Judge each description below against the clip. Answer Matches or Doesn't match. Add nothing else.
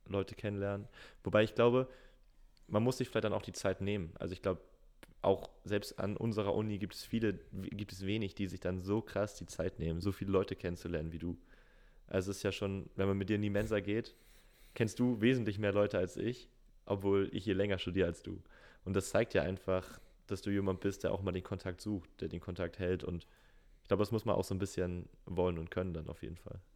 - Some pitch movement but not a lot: Doesn't match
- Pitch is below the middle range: Matches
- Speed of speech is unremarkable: Doesn't match